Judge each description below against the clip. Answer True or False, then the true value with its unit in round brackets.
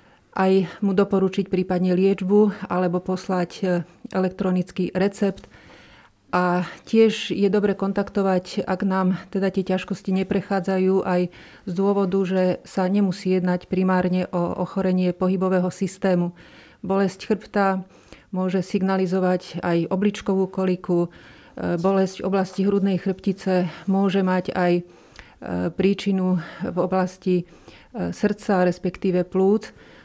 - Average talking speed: False (105 wpm)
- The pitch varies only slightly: True (1.3 semitones)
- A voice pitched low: False (190 Hz)